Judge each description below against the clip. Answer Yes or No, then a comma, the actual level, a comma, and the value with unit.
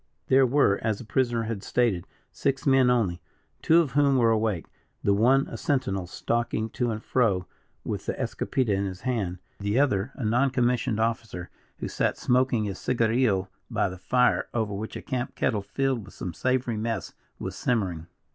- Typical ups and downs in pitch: Yes, average, 4.2 semitones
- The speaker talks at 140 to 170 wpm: No, average, 180 wpm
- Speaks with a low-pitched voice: Yes, low, 115 Hz